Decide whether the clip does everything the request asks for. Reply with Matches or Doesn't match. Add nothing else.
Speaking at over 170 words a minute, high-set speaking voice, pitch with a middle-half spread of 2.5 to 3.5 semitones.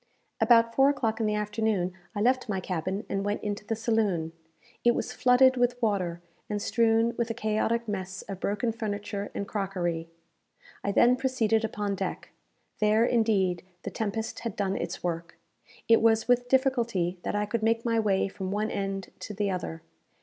Matches